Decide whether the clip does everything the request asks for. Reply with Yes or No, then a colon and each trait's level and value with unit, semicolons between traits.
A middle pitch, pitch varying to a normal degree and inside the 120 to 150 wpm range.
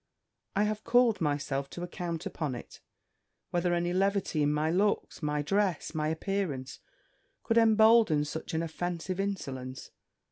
Yes: medium, 175 Hz; average, 5.0 semitones; average, 140 wpm